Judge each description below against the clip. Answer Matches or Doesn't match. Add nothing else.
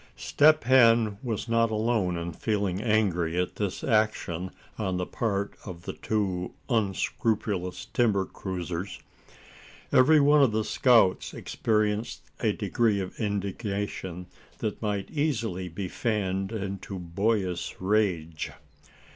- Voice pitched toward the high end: Doesn't match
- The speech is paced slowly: Matches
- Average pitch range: Matches